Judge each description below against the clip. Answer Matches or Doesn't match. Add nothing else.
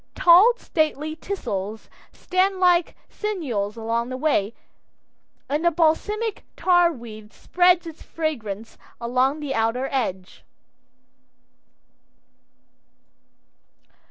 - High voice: Matches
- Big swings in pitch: Matches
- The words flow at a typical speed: Doesn't match